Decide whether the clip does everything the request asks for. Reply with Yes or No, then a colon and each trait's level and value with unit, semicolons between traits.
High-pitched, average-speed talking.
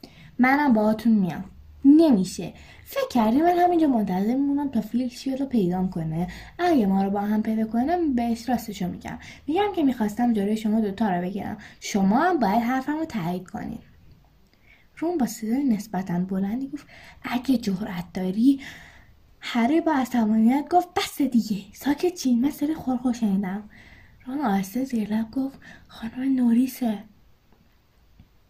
Yes: high, 235 Hz; average, 140 wpm